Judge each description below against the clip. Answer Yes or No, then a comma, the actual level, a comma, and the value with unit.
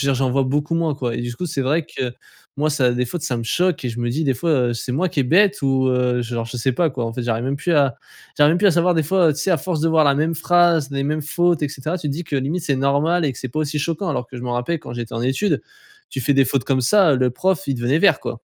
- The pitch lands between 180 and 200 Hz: No, medium, 140 Hz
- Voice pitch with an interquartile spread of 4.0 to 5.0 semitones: Yes, average, 4.6 semitones